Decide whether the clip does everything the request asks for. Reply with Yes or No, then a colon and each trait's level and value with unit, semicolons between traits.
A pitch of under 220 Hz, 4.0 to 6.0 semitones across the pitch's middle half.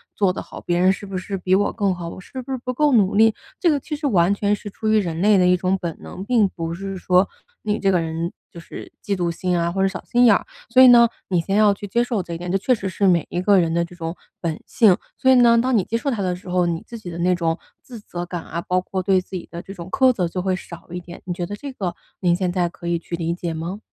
No: medium, 185 Hz; average, 3.3 semitones